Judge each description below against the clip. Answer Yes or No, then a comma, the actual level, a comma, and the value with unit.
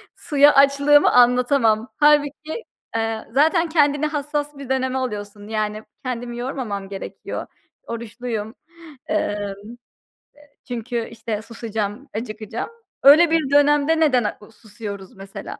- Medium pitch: No, high, 245 Hz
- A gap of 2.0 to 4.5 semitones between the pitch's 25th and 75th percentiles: No, average, 5.0 semitones